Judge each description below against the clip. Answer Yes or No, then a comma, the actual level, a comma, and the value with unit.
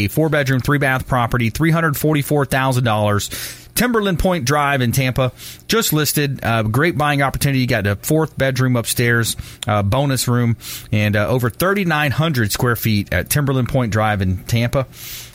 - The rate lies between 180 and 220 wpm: No, average, 150 wpm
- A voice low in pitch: Yes, low, 130 Hz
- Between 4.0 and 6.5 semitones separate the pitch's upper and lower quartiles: Yes, average, 4.3 semitones